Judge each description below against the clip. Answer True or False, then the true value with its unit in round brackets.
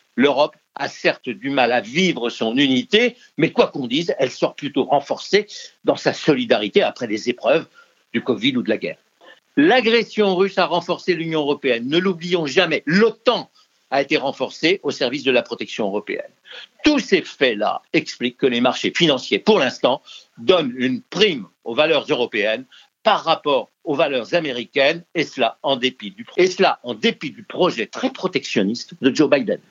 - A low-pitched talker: False (195 Hz)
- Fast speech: False (175 wpm)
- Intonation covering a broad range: True (7.4 semitones)